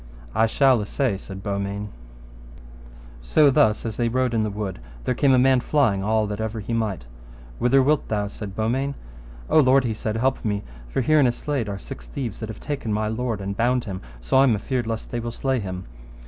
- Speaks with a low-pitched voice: Yes, low, 110 Hz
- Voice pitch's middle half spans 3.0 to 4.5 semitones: Yes, average, 3.9 semitones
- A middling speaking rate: No, fast, 220 wpm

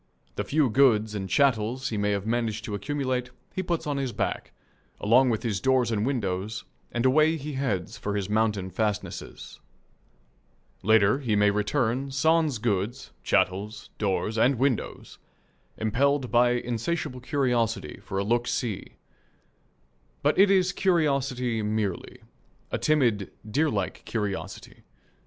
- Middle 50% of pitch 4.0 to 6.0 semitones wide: Yes, average, 4.6 semitones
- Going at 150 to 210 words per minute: No, slow, 135 wpm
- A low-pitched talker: Yes, low, 120 Hz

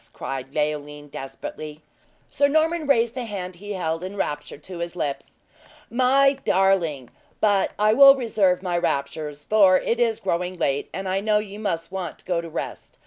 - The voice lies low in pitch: No, medium, 185 Hz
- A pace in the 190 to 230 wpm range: No, average, 175 wpm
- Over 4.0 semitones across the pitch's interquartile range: Yes, wide, 5.5 semitones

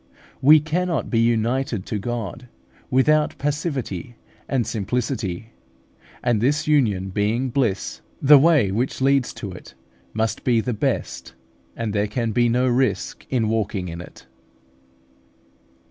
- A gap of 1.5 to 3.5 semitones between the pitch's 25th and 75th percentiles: No, average, 4.2 semitones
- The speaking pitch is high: No, low, 120 Hz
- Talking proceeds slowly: Yes, slow, 130 wpm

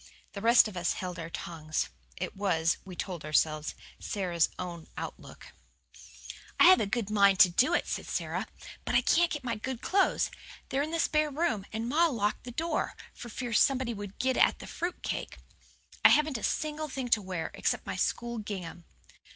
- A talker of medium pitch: No, high, 225 Hz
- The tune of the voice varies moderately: No, wide, 7.1 semitones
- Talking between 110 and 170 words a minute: No, average, 190 wpm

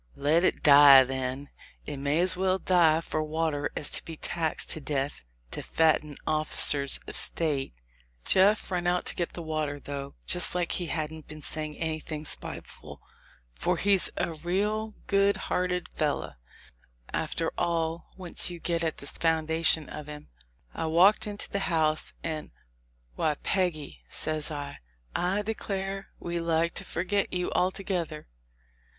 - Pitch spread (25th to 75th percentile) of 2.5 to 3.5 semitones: Yes, average, 3.0 semitones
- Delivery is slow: No, average, 145 wpm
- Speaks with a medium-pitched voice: Yes, medium, 160 Hz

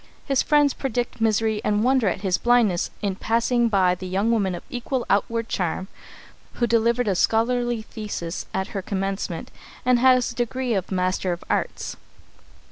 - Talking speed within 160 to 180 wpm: Yes, average, 165 wpm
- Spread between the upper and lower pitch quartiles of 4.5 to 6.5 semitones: No, average, 4.1 semitones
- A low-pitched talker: No, high, 220 Hz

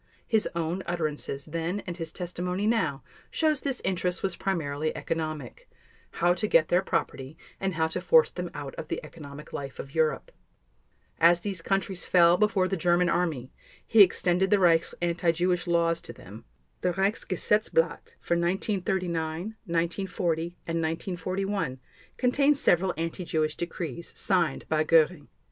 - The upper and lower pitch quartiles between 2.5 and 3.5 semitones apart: Yes, average, 2.9 semitones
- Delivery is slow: No, average, 145 wpm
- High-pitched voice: No, medium, 175 Hz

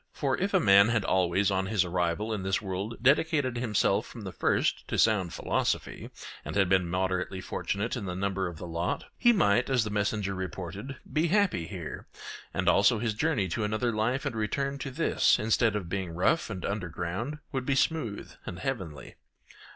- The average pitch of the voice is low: Yes, low, 100 Hz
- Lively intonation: No, average, 4.6 semitones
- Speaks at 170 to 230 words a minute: Yes, average, 190 wpm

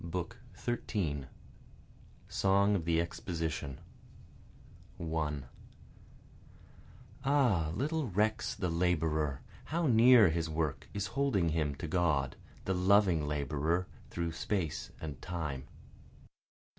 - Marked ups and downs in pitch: No, average, 4.6 semitones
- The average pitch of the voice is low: Yes, very low, 85 Hz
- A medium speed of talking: No, slow, 100 wpm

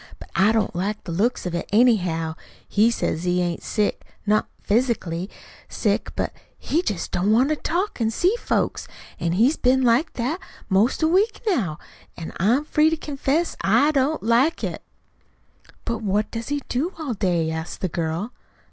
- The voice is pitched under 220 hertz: No, high, 225 Hz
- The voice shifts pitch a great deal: Yes, wide, 7.5 semitones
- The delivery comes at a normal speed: Yes, average, 175 wpm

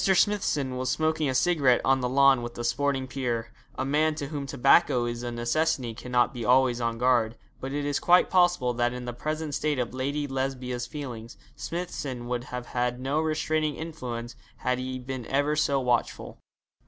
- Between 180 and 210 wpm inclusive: Yes, average, 185 wpm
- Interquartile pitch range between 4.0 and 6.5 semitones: No, average, 3.3 semitones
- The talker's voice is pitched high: No, low, 130 Hz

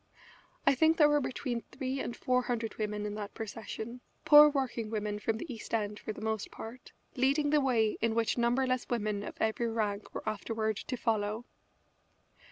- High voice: Yes, high, 230 Hz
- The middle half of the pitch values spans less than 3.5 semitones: Yes, average, 3.0 semitones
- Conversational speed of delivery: Yes, average, 180 wpm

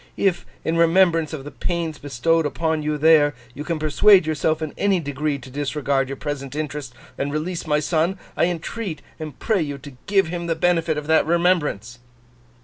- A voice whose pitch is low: No, medium, 155 Hz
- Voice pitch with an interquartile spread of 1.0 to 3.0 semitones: Yes, narrow, 2.5 semitones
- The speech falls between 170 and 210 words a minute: Yes, average, 185 wpm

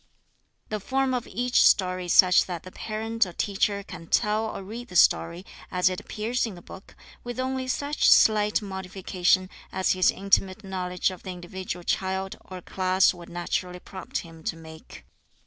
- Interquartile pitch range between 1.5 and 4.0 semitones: Yes, average, 3.0 semitones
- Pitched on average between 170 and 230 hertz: Yes, high, 190 Hz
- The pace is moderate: Yes, average, 175 wpm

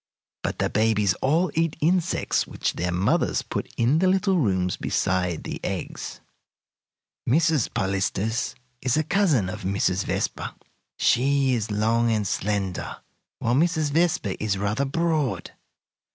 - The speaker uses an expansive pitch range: Yes, wide, 8.0 semitones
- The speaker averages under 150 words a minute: Yes, slow, 135 wpm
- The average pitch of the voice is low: Yes, low, 120 Hz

